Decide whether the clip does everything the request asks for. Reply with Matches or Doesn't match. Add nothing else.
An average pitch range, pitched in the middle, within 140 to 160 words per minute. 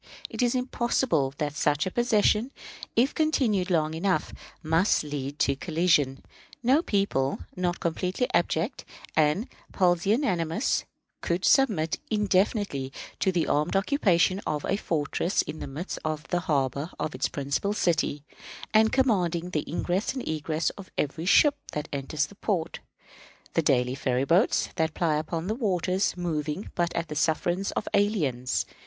Matches